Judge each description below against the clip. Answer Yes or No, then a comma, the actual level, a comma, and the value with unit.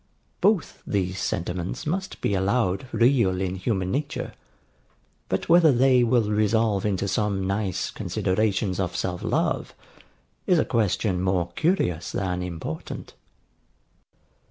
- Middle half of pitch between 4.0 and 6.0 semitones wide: Yes, average, 4.3 semitones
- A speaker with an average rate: No, slow, 120 wpm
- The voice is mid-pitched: No, low, 100 Hz